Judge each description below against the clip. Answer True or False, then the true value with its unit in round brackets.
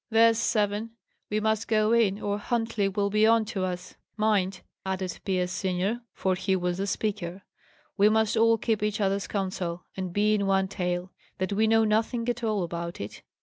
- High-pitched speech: True (205 Hz)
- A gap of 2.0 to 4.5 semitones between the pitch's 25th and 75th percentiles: True (2.7 semitones)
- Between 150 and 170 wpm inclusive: False (190 wpm)